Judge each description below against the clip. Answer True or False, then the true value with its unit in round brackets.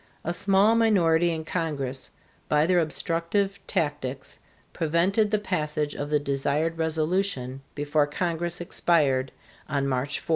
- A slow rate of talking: True (125 wpm)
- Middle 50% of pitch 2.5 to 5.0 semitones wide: True (3.4 semitones)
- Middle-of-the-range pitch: True (160 Hz)